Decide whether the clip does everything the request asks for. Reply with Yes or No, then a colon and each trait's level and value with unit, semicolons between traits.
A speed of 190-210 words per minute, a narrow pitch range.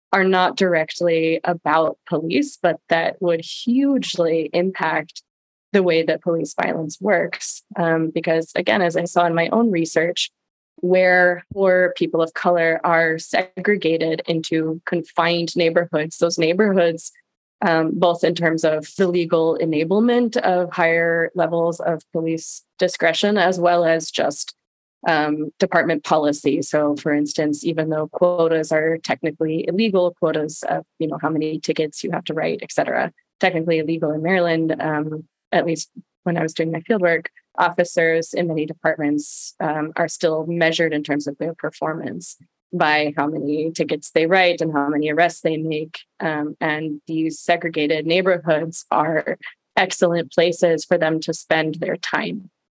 No: average, 150 wpm; narrow, 1.8 semitones